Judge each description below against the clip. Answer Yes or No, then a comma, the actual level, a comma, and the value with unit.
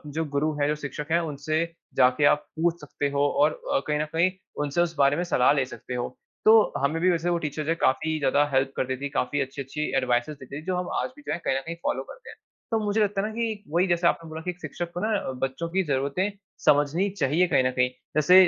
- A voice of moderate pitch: Yes, medium, 150 Hz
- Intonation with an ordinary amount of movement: Yes, average, 3.8 semitones